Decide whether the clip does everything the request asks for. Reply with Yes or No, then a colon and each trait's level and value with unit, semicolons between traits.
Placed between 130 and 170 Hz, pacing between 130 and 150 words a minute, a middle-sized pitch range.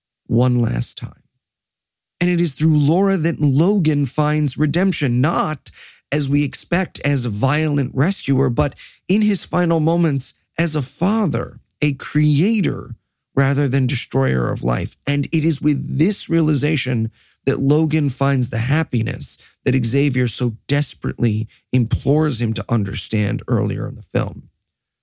Yes: medium, 140 Hz; average, 140 wpm; average, 4.2 semitones